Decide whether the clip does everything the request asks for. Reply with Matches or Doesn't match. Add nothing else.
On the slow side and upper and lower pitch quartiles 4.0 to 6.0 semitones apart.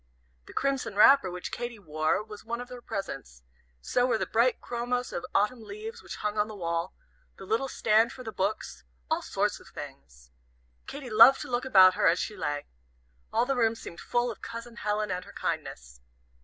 Doesn't match